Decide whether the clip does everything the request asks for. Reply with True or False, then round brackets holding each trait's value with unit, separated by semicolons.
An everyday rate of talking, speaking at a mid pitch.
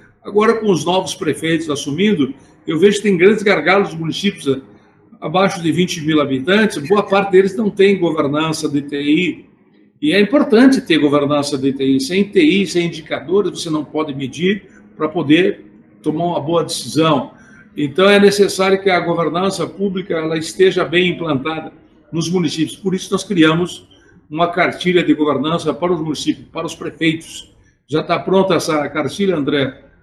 True (160 wpm; 165 Hz)